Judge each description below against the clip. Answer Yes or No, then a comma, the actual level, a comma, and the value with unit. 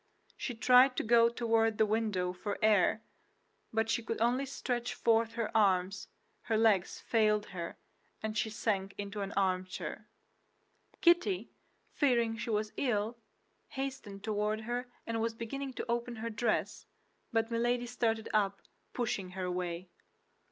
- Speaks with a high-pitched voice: Yes, high, 225 Hz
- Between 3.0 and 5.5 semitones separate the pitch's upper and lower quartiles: No, narrow, 2.5 semitones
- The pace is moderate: Yes, average, 145 wpm